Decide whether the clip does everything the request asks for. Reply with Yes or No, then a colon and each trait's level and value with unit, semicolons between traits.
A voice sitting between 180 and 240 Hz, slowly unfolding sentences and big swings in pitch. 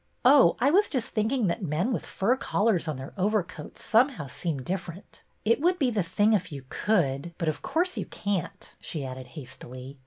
No: medium, 185 Hz; average, 195 wpm; wide, 7.5 semitones